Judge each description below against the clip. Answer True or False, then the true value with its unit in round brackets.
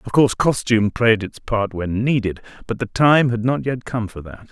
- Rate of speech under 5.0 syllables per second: False (5.1 syllables/s)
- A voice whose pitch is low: True (115 Hz)